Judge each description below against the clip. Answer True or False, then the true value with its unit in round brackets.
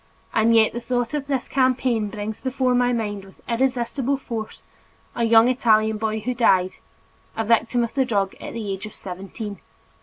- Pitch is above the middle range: True (230 Hz)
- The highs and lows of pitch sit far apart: False (2.6 semitones)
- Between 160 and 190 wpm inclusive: True (180 wpm)